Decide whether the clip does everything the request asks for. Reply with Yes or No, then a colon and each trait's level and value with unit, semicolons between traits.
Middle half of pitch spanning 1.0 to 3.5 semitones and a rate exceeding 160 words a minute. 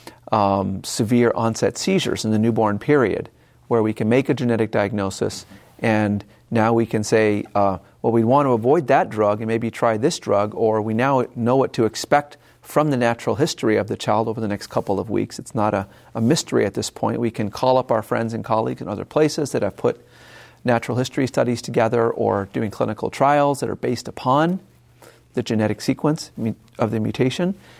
Yes: average, 2.9 semitones; average, 200 wpm